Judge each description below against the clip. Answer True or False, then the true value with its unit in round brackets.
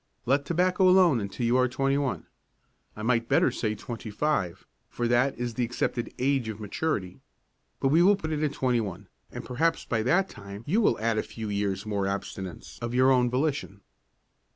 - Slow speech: False (195 wpm)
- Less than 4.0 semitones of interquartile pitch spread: False (4.9 semitones)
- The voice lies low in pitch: True (120 Hz)